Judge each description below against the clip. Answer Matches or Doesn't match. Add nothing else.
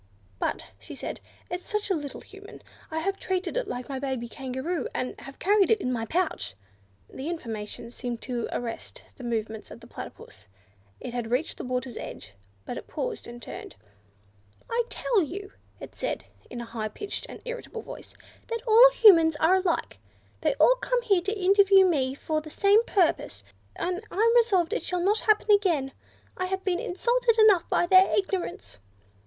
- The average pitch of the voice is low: Doesn't match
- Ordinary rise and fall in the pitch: Doesn't match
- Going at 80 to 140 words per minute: Doesn't match